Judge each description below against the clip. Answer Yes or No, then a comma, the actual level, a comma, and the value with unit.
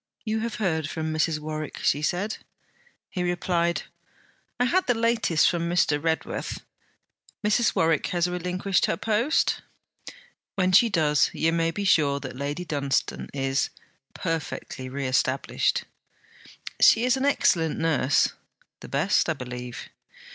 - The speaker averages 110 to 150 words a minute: Yes, slow, 135 wpm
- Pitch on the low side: No, medium, 165 Hz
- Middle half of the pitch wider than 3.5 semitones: Yes, average, 4.9 semitones